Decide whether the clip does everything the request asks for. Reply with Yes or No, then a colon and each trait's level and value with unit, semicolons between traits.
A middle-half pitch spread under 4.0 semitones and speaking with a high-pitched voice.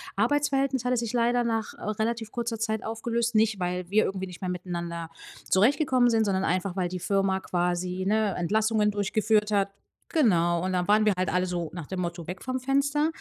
No: average, 4.3 semitones; high, 210 Hz